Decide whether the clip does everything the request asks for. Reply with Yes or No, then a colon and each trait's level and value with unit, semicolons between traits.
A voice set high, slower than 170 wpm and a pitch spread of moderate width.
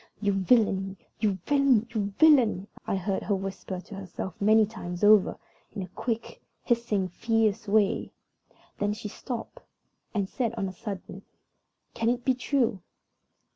Yes: high, 210 Hz; average, 145 wpm; average, 3.1 semitones